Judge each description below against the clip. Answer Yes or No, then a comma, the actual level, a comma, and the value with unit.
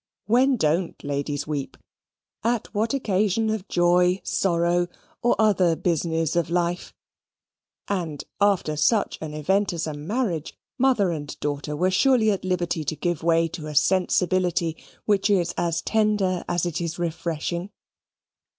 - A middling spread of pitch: Yes, average, 3.7 semitones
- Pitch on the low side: No, medium, 175 Hz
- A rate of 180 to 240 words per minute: No, average, 140 wpm